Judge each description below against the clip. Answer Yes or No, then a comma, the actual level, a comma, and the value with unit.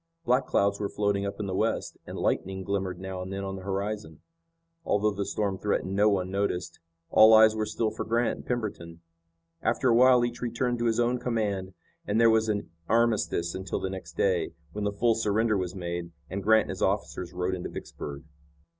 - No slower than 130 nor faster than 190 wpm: No, fast, 205 wpm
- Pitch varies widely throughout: No, average, 2.9 semitones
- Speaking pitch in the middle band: No, low, 100 Hz